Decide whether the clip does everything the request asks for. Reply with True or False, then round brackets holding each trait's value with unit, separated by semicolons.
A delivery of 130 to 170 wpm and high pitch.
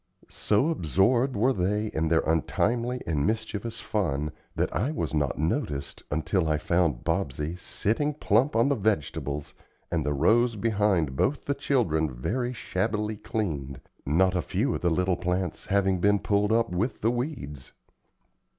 False (155 wpm; 95 Hz)